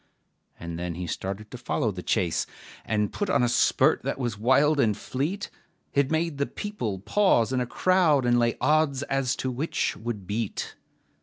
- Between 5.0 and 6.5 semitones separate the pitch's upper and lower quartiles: Yes, wide, 5.6 semitones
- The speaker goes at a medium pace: Yes, average, 180 wpm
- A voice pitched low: Yes, low, 125 Hz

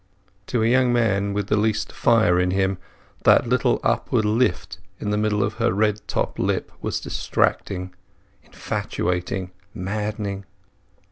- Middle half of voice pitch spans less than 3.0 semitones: Yes, narrow, 2.5 semitones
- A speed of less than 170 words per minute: Yes, average, 140 wpm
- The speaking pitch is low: Yes, low, 105 Hz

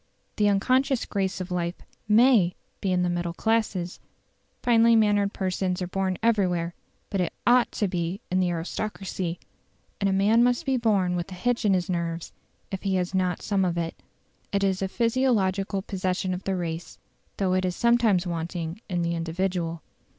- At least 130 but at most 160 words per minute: No, average, 180 wpm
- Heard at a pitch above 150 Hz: Yes, high, 190 Hz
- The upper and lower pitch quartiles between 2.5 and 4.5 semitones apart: Yes, average, 2.9 semitones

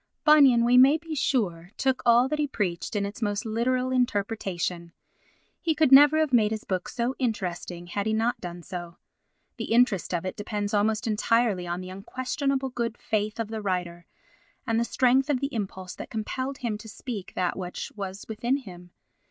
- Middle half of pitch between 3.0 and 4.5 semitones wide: No, average, 5.3 semitones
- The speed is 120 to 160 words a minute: No, average, 185 wpm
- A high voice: Yes, high, 220 Hz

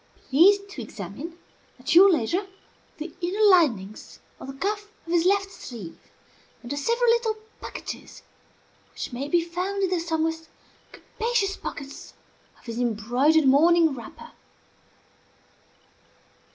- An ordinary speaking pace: No, slow, 125 wpm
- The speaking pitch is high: Yes, very high, 325 Hz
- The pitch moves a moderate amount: No, wide, 6.6 semitones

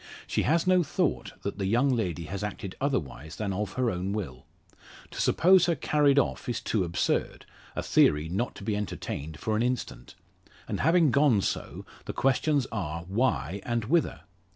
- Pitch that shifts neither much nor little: No, wide, 6.9 semitones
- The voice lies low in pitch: Yes, low, 110 Hz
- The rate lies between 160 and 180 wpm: Yes, average, 175 wpm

